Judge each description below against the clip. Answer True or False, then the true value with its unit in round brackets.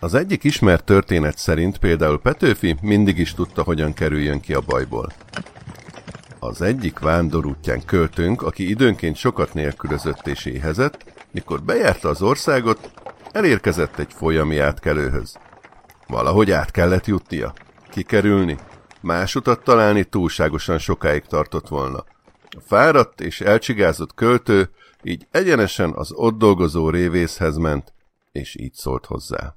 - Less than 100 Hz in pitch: True (85 Hz)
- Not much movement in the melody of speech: False (4.3 semitones)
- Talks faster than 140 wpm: False (125 wpm)